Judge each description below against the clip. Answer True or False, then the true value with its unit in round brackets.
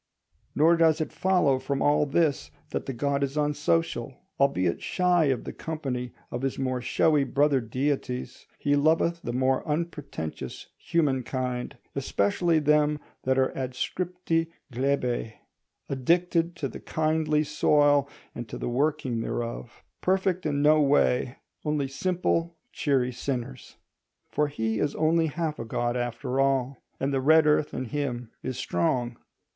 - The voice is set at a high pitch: False (140 Hz)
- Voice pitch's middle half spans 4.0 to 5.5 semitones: False (3.6 semitones)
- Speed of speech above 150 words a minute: False (140 wpm)